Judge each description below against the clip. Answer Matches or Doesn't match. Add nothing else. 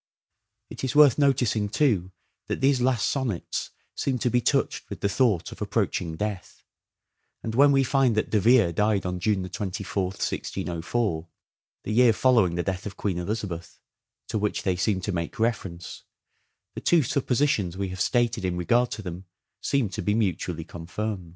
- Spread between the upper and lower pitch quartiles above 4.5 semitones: Matches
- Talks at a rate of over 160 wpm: Matches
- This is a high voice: Doesn't match